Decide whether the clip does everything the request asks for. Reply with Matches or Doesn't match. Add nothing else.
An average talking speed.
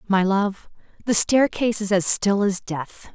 Matches